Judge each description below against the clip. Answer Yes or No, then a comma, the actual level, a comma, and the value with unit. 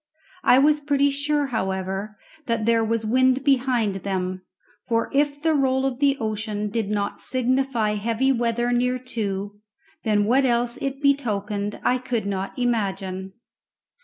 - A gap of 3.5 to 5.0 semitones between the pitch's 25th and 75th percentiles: Yes, average, 4.3 semitones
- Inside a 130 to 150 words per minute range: Yes, average, 145 wpm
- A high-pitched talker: Yes, high, 235 Hz